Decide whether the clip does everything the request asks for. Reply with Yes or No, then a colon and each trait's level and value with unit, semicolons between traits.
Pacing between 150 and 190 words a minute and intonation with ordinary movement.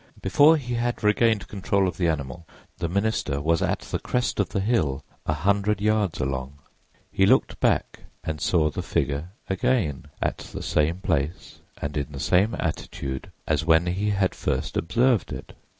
No: average, 170 wpm; wide, 5.7 semitones